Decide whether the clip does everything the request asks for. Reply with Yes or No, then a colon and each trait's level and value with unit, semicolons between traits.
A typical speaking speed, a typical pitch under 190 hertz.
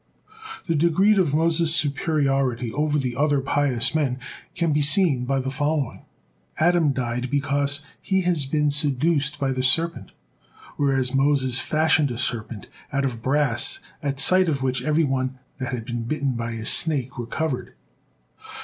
Yes: average, 150 wpm; medium, 140 Hz